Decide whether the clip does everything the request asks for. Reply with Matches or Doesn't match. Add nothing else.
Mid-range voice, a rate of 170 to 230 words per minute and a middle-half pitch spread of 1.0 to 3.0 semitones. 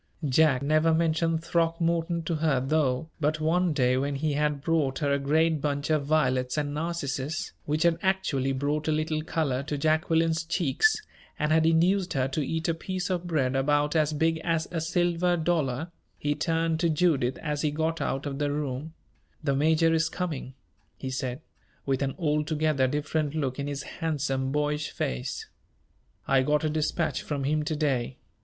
Matches